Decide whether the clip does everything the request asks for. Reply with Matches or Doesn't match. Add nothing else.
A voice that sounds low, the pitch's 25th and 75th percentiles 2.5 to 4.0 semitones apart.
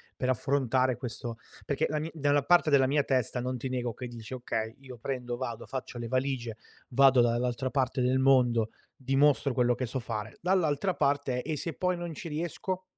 Matches